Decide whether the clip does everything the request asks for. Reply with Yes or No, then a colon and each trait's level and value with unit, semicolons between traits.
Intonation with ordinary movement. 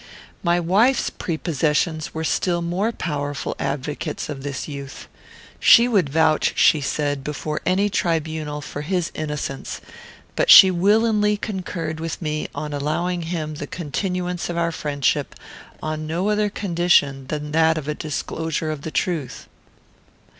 Yes: average, 3.3 semitones